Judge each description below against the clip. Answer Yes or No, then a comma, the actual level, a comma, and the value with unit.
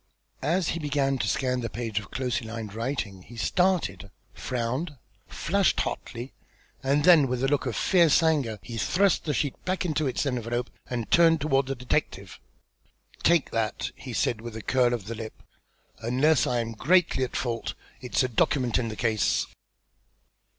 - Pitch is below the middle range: Yes, low, 125 Hz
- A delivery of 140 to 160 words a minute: No, average, 170 wpm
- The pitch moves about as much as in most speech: Yes, average, 4.5 semitones